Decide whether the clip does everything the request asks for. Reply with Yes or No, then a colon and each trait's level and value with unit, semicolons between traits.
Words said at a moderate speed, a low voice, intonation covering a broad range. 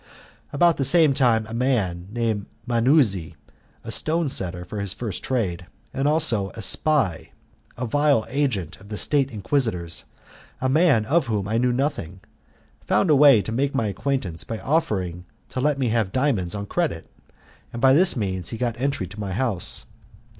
Yes: average, 175 wpm; low, 115 Hz; wide, 6.0 semitones